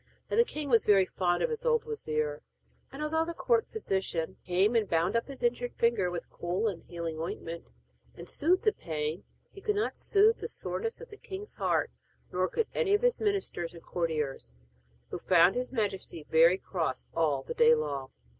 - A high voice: Yes, high, 195 Hz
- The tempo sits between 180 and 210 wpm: Yes, average, 195 wpm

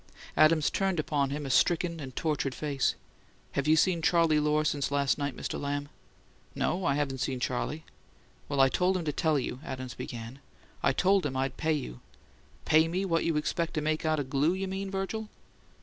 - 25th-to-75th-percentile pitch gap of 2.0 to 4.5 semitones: Yes, average, 3.4 semitones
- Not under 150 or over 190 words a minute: No, average, 200 wpm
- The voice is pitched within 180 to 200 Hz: No, medium, 150 Hz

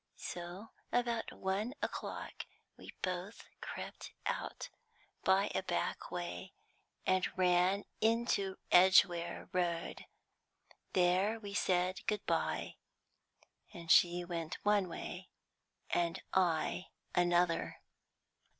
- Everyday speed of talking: No, slow, 95 wpm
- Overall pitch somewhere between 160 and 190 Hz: Yes, medium, 185 Hz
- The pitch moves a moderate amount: No, narrow, 2.2 semitones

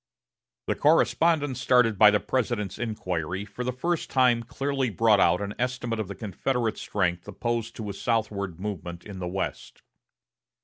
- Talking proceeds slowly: No, average, 160 wpm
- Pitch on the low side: Yes, low, 110 Hz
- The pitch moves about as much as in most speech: Yes, average, 3.9 semitones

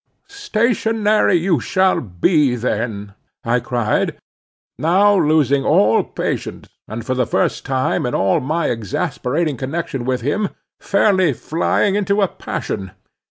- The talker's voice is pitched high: No, medium, 145 Hz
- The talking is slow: Yes, slow, 125 wpm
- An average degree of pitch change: No, wide, 7.8 semitones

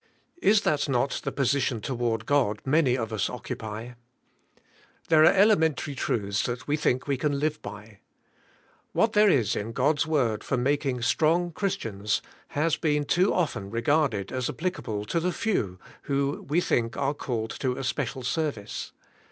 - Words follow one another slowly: No, average, 165 wpm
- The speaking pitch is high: No, low, 135 Hz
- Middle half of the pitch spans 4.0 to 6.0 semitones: Yes, average, 5.2 semitones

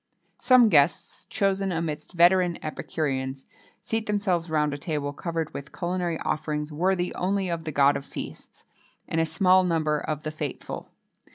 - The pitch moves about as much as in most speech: Yes, average, 3.4 semitones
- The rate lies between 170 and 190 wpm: No, average, 155 wpm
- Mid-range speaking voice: Yes, medium, 165 Hz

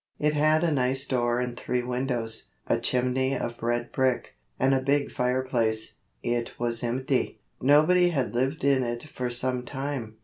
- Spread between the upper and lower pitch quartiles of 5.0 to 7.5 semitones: No, narrow, 2.4 semitones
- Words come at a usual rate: Yes, average, 165 wpm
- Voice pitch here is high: No, low, 125 Hz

